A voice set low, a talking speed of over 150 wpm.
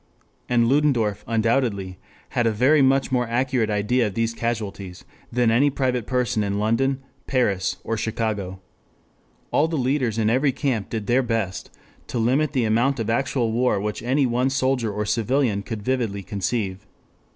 Yes: low, 115 Hz; average, 165 wpm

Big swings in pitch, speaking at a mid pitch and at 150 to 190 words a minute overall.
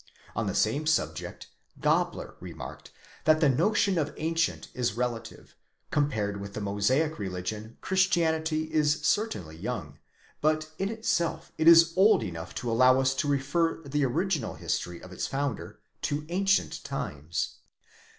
No: wide, 6.8 semitones; medium, 145 Hz; average, 140 wpm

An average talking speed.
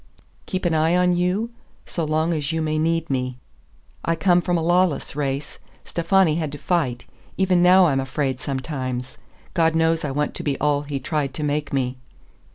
Yes: average, 185 wpm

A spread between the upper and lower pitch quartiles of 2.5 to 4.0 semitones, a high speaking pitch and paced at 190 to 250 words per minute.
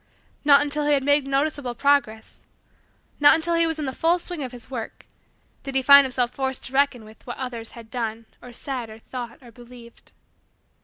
Yes: average, 3.2 semitones; very high, 265 Hz; average, 200 wpm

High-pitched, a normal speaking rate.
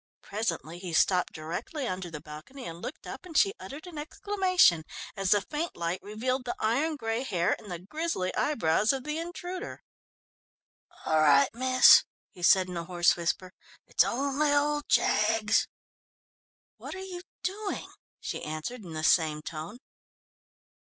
Yes: high, 220 Hz; average, 155 wpm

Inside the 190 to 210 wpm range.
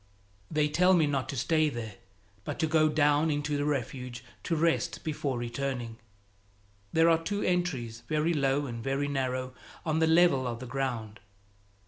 No: average, 165 wpm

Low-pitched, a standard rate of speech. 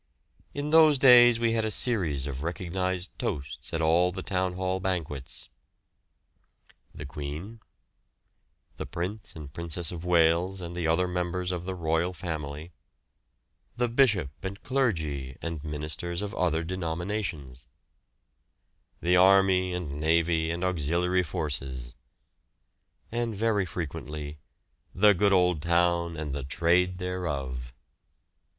No: very low, 85 Hz; slow, 125 wpm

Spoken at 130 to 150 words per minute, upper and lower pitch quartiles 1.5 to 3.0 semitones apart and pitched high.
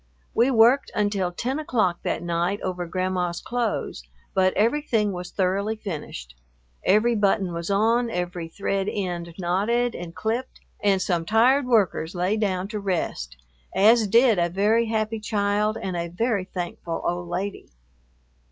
No: average, 145 wpm; average, 4.0 semitones; high, 200 Hz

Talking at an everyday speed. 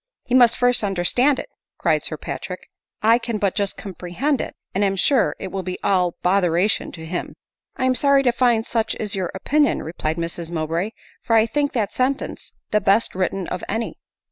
No: fast, 210 wpm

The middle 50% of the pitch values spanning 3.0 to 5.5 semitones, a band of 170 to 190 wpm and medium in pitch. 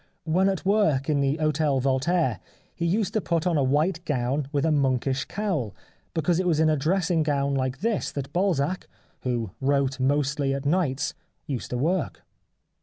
Yes: average, 4.0 semitones; average, 180 wpm; medium, 150 Hz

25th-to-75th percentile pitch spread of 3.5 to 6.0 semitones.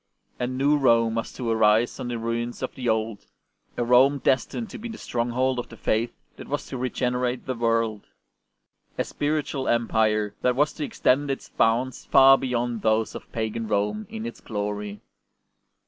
No: average, 2.8 semitones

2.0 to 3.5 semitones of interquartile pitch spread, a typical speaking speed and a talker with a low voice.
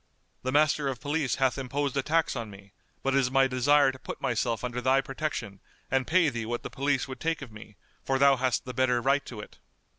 No: narrow, 2.4 semitones; fast, 235 wpm; low, 130 Hz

